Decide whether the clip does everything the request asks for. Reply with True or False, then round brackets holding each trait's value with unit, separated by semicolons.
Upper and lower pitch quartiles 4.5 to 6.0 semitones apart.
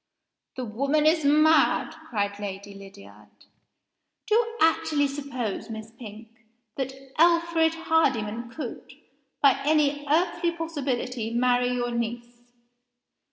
True (5.2 semitones)